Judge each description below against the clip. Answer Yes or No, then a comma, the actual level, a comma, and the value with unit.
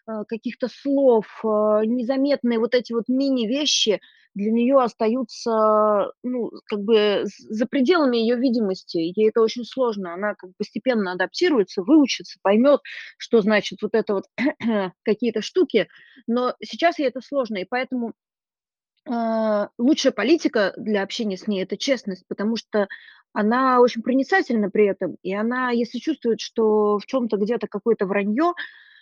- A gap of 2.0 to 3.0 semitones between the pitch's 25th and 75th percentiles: No, average, 3.8 semitones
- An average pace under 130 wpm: No, average, 140 wpm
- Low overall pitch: No, high, 230 Hz